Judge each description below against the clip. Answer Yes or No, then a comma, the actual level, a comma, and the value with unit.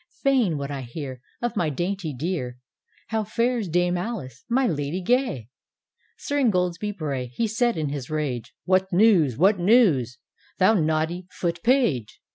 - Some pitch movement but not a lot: No, wide, 7.4 semitones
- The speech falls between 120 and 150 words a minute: No, average, 160 wpm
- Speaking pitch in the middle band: Yes, medium, 175 Hz